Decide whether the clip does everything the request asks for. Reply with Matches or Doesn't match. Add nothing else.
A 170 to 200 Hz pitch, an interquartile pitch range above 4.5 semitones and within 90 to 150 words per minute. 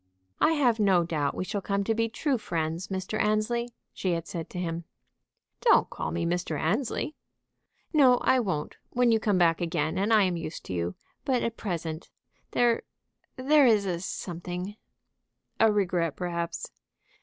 Doesn't match